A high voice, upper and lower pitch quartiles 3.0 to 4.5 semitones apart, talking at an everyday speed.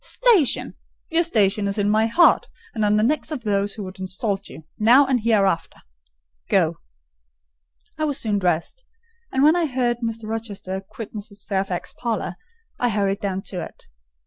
Yes: high, 210 Hz; average, 3.8 semitones; average, 160 wpm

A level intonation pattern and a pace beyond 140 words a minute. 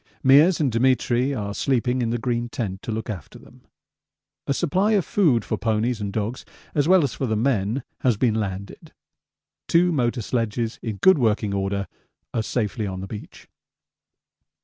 No: average, 4.1 semitones; average, 170 wpm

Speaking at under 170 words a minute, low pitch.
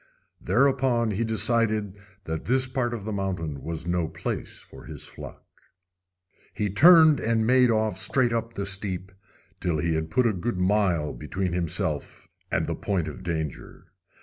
Yes: average, 160 wpm; low, 100 Hz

